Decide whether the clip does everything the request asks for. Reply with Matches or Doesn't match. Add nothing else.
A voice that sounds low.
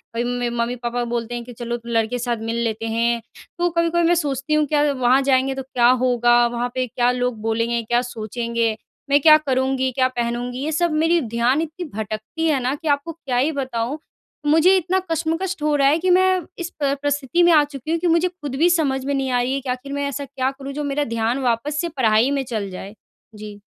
Doesn't match